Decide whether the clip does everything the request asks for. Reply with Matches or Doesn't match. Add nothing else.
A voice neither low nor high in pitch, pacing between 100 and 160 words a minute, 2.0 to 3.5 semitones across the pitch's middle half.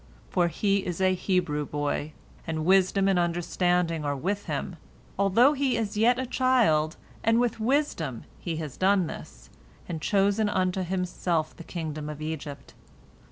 Doesn't match